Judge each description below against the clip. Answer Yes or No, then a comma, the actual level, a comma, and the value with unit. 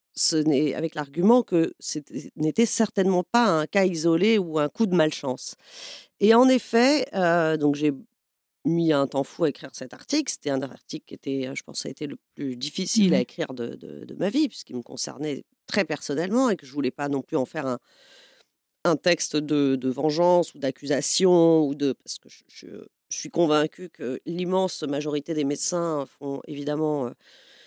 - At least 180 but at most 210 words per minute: Yes, average, 195 wpm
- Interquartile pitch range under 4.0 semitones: No, average, 4.7 semitones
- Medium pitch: Yes, medium, 155 Hz